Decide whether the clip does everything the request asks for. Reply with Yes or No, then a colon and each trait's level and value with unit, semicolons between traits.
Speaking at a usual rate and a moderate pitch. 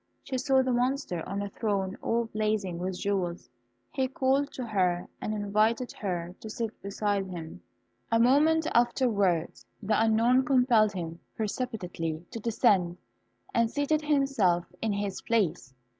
No: average, 145 wpm; high, 215 Hz